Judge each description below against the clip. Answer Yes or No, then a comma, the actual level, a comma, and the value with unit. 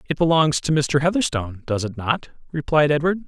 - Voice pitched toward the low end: No, medium, 150 Hz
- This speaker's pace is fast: No, average, 185 wpm